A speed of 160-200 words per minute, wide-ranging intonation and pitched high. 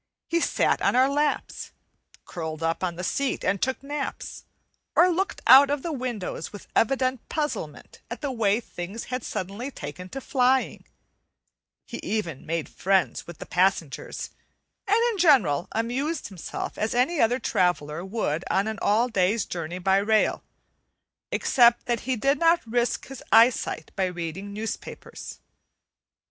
No: average, 150 wpm; wide, 6.4 semitones; high, 225 Hz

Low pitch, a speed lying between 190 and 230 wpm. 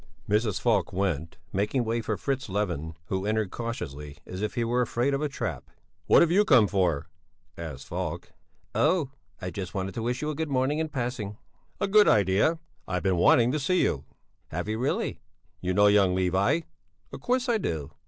Yes: low, 105 Hz; average, 195 wpm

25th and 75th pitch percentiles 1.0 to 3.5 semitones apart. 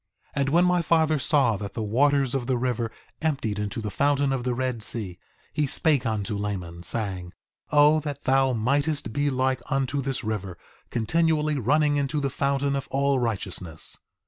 No: average, 4.6 semitones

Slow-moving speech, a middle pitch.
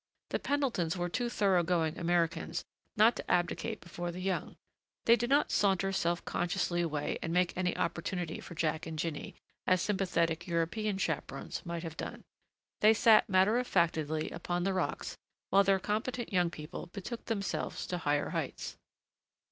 No: average, 165 wpm; medium, 180 Hz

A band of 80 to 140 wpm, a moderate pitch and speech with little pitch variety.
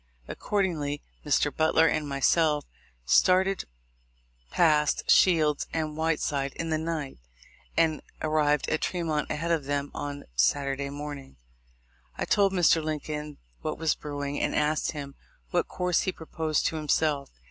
Yes: slow, 135 wpm; medium, 150 Hz; narrow, 2.2 semitones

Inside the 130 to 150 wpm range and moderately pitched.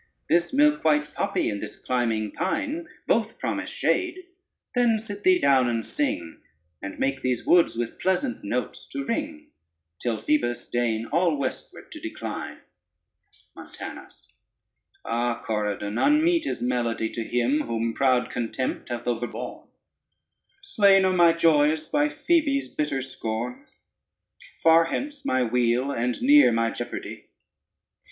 Yes: average, 140 wpm; medium, 145 Hz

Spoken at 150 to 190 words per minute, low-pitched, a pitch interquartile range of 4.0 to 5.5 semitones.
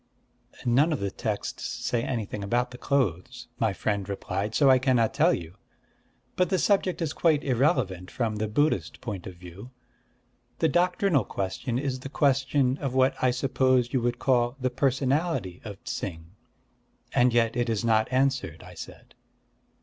Yes: average, 165 wpm; low, 125 Hz; average, 5.1 semitones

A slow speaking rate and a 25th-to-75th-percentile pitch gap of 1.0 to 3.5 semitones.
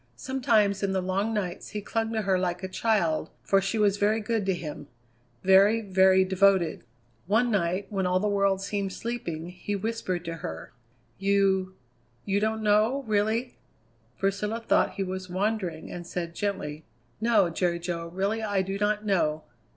No: average, 165 wpm; narrow, 2.6 semitones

